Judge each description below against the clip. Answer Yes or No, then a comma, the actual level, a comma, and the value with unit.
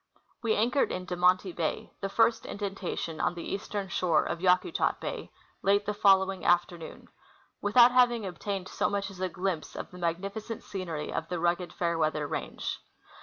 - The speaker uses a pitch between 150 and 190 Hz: Yes, medium, 185 Hz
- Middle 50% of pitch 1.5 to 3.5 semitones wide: Yes, average, 2.8 semitones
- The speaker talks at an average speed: Yes, average, 170 wpm